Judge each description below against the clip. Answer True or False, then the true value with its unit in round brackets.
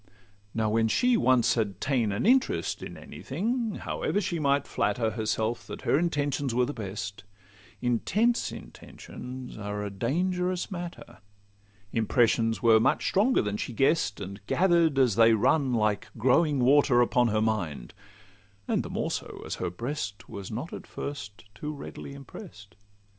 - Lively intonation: True (6.1 semitones)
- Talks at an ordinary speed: True (155 wpm)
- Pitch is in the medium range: False (125 Hz)